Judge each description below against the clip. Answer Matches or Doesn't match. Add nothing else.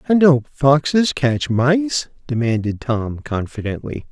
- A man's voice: Matches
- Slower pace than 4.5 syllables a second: Matches